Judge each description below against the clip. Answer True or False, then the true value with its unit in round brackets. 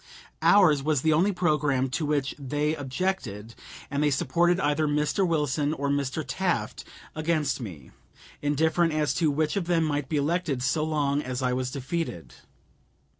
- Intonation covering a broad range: False (2.8 semitones)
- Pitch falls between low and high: True (150 Hz)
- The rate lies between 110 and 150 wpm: False (160 wpm)